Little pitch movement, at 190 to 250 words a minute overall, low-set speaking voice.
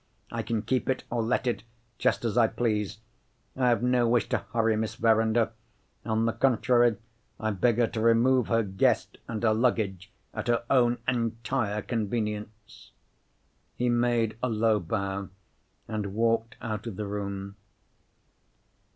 No: narrow, 2.0 semitones; average, 150 wpm; low, 115 Hz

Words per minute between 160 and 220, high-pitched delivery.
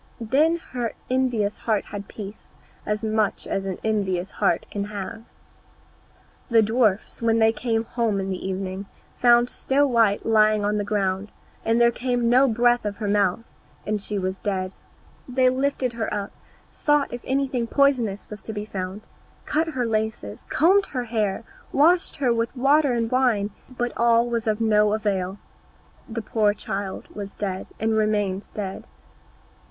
Yes: average, 165 wpm; high, 220 Hz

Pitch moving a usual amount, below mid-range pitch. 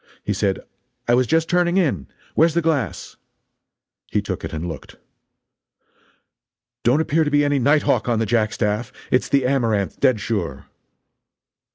No: wide, 6.0 semitones; low, 125 Hz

